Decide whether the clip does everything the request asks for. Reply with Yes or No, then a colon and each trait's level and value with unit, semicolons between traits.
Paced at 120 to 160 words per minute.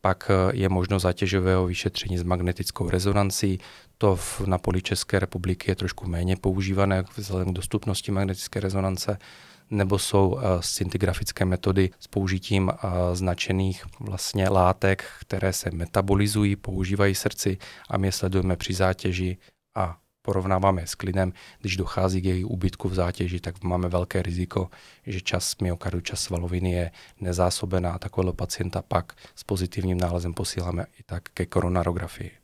Yes: average, 140 wpm